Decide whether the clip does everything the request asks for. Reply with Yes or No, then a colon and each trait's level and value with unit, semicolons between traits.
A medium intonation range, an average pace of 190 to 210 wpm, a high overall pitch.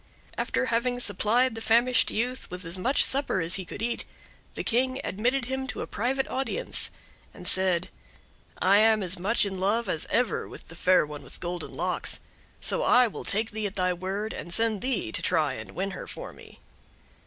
Yes: average, 5.0 semitones; average, 200 wpm; high, 215 Hz